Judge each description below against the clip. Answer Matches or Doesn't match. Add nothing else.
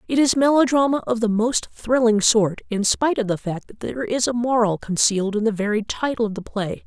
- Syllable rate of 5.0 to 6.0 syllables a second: Matches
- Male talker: Doesn't match